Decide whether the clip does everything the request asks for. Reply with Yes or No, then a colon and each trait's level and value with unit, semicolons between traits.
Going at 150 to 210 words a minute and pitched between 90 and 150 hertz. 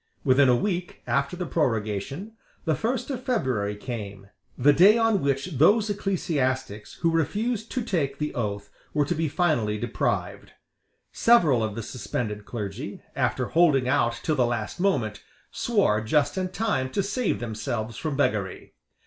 Yes: average, 155 wpm; medium, 140 Hz